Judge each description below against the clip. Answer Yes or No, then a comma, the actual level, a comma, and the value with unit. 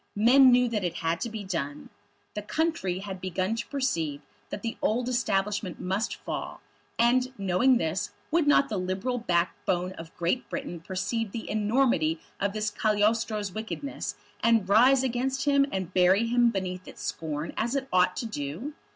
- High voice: Yes, high, 210 Hz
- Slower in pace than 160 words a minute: No, average, 170 wpm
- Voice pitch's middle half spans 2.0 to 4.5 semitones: No, average, 5.0 semitones